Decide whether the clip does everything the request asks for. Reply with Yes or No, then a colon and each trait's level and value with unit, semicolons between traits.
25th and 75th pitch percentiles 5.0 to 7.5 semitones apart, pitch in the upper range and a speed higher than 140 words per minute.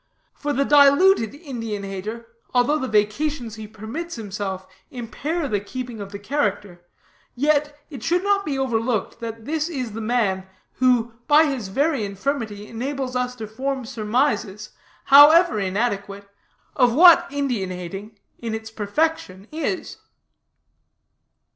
No: wide, 5.4 semitones; high, 240 Hz; slow, 135 wpm